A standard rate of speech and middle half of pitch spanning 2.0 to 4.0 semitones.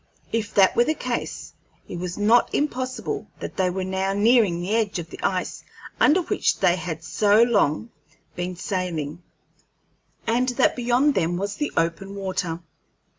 No: average, 160 wpm; average, 4.9 semitones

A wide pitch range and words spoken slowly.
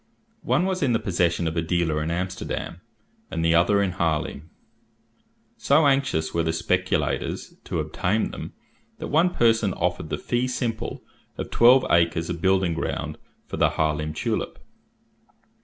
No: wide, 6.1 semitones; average, 155 wpm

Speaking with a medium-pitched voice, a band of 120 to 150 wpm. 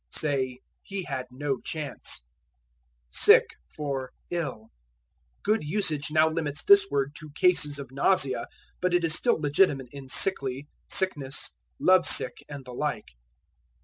Yes: medium, 145 Hz; slow, 135 wpm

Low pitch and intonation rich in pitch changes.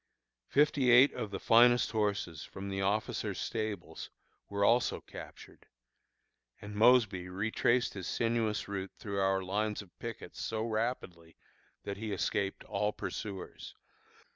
No: low, 105 Hz; average, 2.8 semitones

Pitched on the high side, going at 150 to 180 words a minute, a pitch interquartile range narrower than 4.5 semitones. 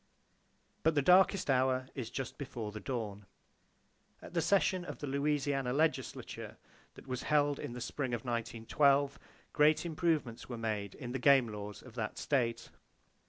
No: low, 130 Hz; average, 160 wpm; average, 4.1 semitones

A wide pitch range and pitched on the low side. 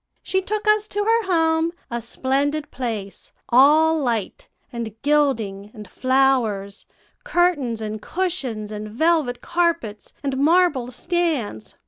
No: wide, 7.2 semitones; very high, 270 Hz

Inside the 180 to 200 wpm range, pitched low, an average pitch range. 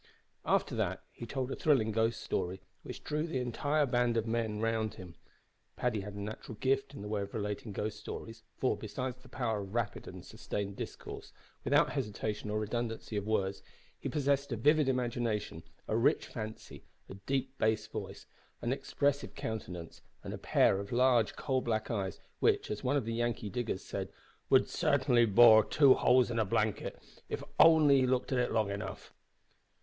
Yes: average, 185 wpm; low, 115 Hz; average, 3.6 semitones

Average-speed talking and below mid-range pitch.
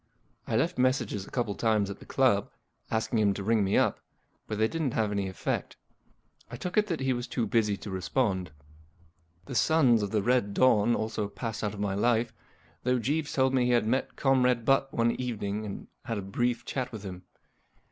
No: fast, 210 wpm; low, 115 Hz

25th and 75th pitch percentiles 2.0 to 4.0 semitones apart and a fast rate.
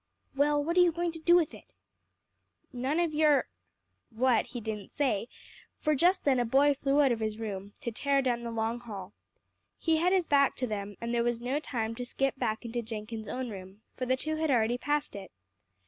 No: average, 4.6 semitones; fast, 220 wpm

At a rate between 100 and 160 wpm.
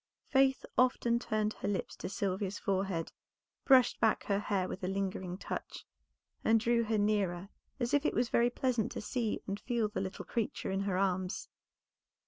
No: average, 175 wpm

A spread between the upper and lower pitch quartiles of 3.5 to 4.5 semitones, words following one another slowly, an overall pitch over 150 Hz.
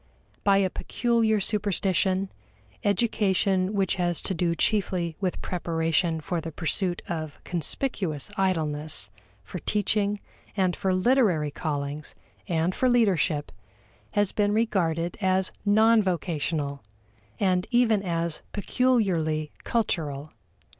Yes: average, 4.1 semitones; slow, 110 wpm; medium, 185 Hz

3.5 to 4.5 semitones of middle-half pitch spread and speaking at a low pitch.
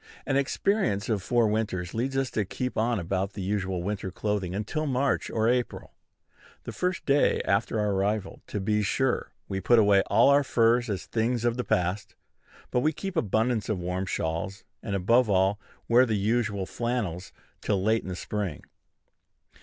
Yes: average, 3.8 semitones; low, 110 Hz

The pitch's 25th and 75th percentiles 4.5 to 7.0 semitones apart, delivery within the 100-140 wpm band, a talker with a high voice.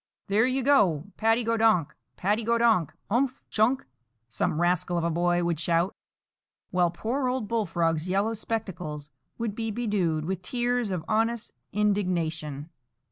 Yes: average, 5.0 semitones; slow, 135 wpm; high, 200 Hz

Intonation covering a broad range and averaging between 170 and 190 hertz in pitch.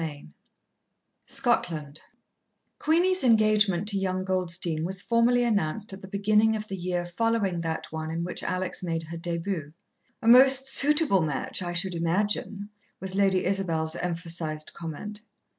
No: average, 4.1 semitones; medium, 185 Hz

